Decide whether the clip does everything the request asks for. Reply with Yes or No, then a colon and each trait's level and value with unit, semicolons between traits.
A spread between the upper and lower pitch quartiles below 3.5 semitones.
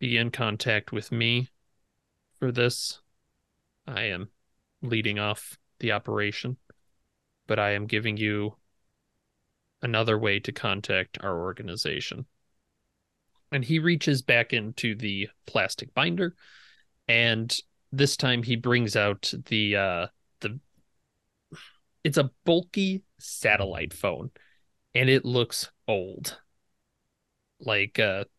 No: average, 3.9 semitones